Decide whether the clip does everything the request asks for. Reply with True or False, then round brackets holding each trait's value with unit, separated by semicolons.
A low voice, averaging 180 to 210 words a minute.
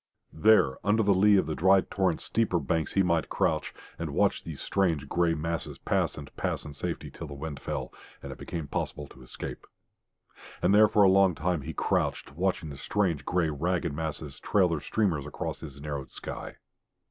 True (80 Hz; 195 wpm)